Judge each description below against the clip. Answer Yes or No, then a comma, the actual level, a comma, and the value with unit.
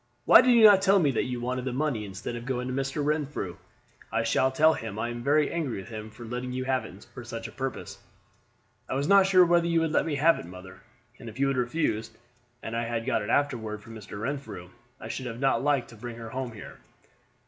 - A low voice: Yes, low, 125 Hz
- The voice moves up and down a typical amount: Yes, average, 4.3 semitones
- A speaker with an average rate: No, fast, 245 wpm